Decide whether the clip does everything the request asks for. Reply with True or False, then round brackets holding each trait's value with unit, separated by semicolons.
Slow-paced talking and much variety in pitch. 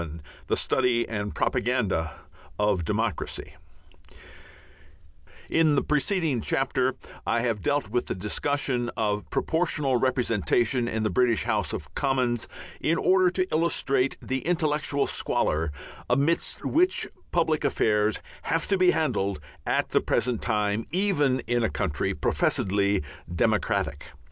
True (125 wpm; 5.9 semitones)